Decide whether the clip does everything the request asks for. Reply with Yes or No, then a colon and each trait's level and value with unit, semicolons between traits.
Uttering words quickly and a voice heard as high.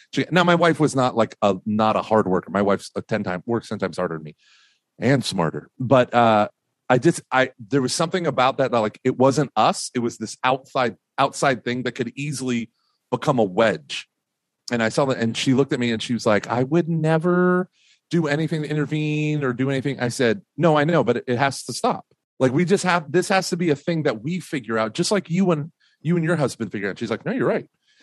No: fast, 245 wpm; low, 130 Hz